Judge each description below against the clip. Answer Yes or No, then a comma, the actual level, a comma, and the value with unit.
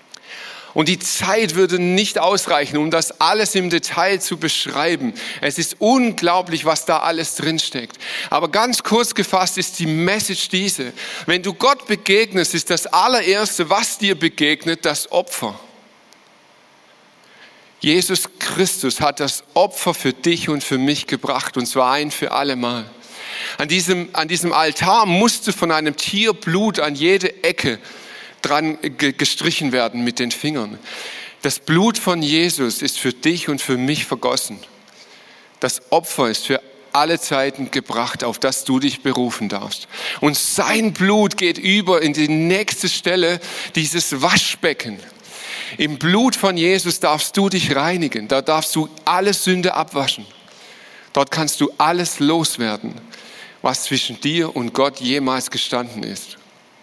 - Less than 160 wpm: Yes, average, 145 wpm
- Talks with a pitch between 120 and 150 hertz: No, medium, 165 Hz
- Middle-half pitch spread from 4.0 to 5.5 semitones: Yes, average, 4.8 semitones